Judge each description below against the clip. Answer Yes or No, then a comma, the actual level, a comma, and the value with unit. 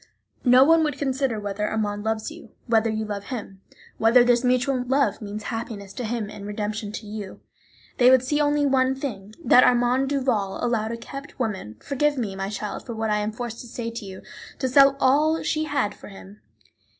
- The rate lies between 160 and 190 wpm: No, average, 200 wpm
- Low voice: No, high, 235 Hz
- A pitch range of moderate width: Yes, average, 4.0 semitones